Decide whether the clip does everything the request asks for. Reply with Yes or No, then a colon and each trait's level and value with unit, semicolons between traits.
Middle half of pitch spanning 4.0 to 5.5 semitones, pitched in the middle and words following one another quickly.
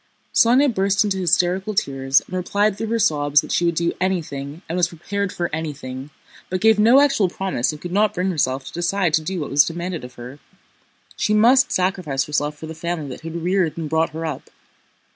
Yes: average, 4.4 semitones; medium, 175 Hz; fast, 210 wpm